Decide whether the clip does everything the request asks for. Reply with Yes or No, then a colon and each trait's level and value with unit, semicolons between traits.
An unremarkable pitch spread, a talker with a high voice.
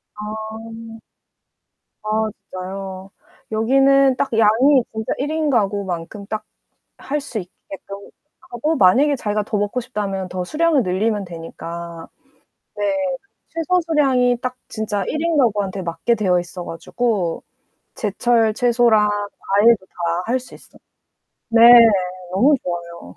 Yes: average, 4.6 semitones; high, 215 Hz